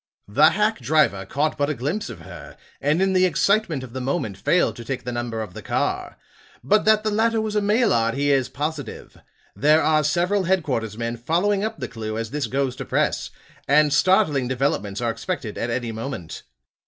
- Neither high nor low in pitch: Yes, medium, 145 Hz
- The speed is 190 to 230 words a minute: Yes, average, 200 wpm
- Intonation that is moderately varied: No, wide, 7.6 semitones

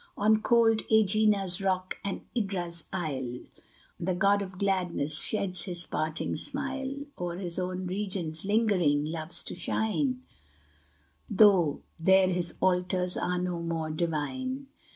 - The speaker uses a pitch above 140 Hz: Yes, medium, 185 Hz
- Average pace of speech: No, slow, 125 wpm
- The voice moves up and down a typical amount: Yes, average, 3.6 semitones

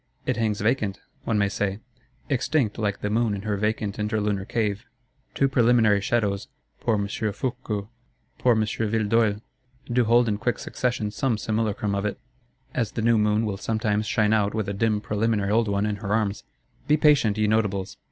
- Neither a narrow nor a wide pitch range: No, narrow, 2.0 semitones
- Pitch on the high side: No, low, 110 Hz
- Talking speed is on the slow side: No, average, 175 wpm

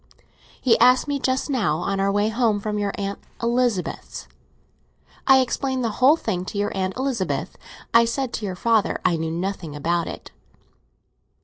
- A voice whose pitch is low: No, high, 215 Hz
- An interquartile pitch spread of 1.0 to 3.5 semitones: No, average, 4.9 semitones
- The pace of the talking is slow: No, average, 170 wpm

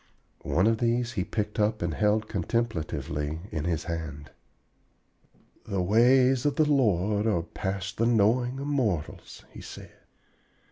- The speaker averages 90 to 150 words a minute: Yes, average, 140 wpm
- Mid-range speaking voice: No, low, 105 Hz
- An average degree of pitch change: No, wide, 5.7 semitones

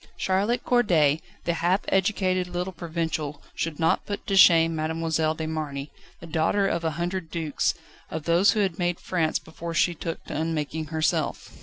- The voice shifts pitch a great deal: No, narrow, 2.5 semitones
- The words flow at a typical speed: Yes, average, 170 wpm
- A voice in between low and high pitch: Yes, medium, 165 Hz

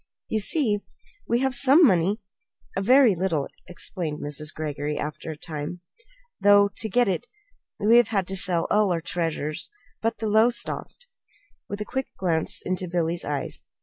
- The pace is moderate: Yes, average, 160 wpm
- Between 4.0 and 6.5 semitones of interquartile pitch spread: Yes, average, 5.1 semitones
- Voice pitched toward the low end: No, high, 190 Hz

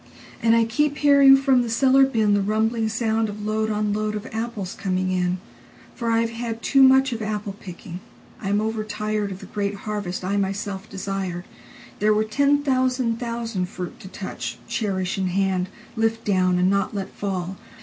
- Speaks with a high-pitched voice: Yes, high, 210 Hz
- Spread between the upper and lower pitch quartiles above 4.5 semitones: No, average, 3.1 semitones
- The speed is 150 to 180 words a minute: Yes, average, 160 wpm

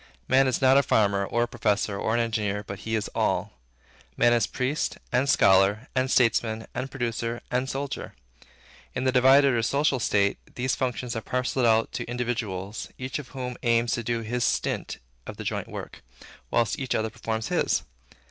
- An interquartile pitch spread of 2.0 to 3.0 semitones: Yes, narrow, 2.6 semitones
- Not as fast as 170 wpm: No, average, 185 wpm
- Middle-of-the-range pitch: No, low, 120 Hz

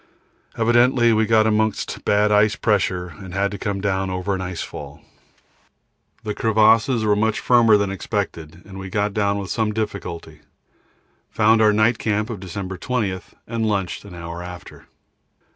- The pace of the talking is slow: No, average, 160 wpm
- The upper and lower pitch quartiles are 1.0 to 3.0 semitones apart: Yes, narrow, 2.5 semitones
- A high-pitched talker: No, low, 105 Hz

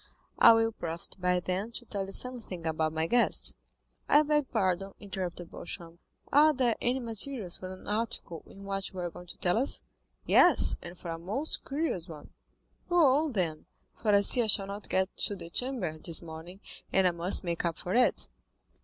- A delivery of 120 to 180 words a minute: No, average, 195 wpm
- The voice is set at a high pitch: Yes, high, 195 Hz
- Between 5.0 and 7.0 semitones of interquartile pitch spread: Yes, wide, 5.4 semitones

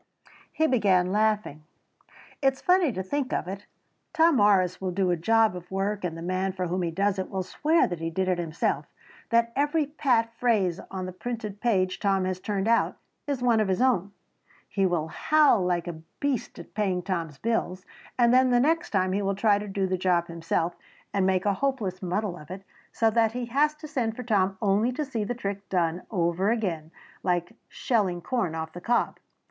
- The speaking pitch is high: Yes, high, 195 Hz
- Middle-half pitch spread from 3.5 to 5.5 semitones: Yes, average, 4.5 semitones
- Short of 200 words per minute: No, fast, 205 wpm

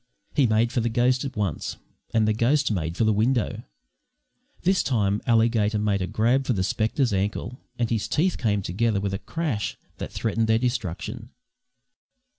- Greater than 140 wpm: Yes, average, 175 wpm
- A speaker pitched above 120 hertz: No, low, 110 Hz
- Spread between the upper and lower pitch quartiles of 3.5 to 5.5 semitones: No, average, 3.0 semitones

